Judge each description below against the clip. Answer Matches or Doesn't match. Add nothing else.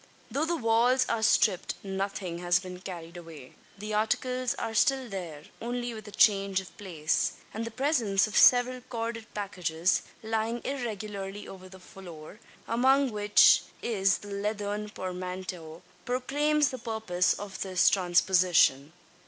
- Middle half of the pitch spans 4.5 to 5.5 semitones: Doesn't match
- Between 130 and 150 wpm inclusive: Matches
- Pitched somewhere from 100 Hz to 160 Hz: Doesn't match